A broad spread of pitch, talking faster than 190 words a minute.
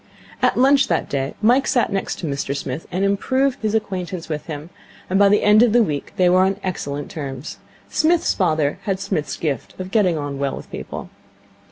Yes: wide, 6.1 semitones; average, 200 wpm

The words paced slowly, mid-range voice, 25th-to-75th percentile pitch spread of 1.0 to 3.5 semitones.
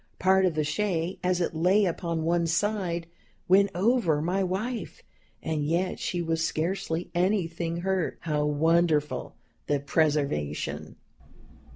Yes: slow, 130 wpm; medium, 170 Hz; average, 2.9 semitones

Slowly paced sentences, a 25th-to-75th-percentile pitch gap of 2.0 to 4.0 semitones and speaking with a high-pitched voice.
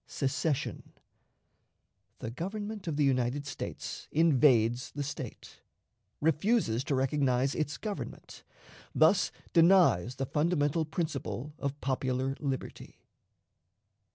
No: slow, 100 wpm; average, 3.7 semitones; medium, 145 Hz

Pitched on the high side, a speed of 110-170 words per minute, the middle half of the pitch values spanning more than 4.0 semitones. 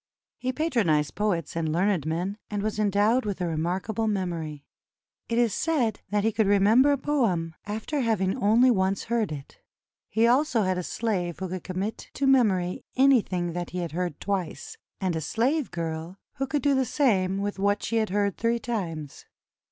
No: high, 200 Hz; average, 185 wpm; average, 4.7 semitones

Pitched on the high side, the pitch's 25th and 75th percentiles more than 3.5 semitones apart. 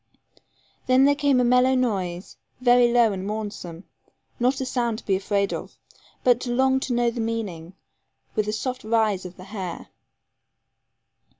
Yes: high, 230 Hz; average, 4.1 semitones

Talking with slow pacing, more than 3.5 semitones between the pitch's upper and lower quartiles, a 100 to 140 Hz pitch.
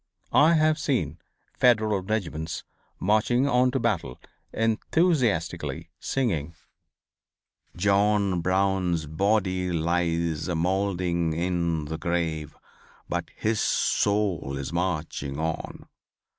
No: slow, 95 wpm; average, 4.4 semitones; very low, 90 Hz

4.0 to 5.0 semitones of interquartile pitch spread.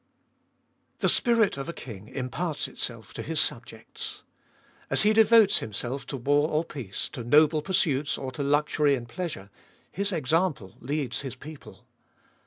Yes: average, 4.6 semitones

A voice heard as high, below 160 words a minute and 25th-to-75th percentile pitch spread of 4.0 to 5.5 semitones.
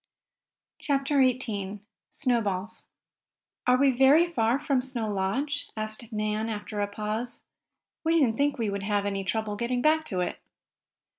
Yes: high, 230 Hz; average, 145 wpm; average, 4.6 semitones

